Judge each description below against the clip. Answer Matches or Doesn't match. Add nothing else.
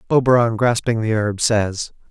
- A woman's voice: Doesn't match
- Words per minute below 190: Matches